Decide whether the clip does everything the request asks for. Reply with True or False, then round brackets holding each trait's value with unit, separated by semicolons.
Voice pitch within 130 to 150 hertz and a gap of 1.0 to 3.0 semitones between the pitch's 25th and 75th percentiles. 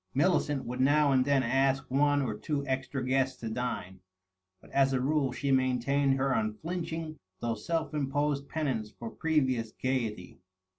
True (135 Hz; 2.5 semitones)